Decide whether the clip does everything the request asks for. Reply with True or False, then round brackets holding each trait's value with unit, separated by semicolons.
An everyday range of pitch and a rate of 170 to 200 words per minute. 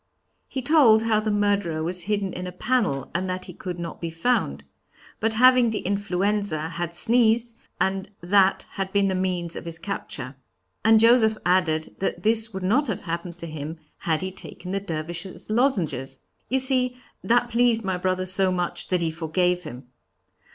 True (4.3 semitones; 180 wpm)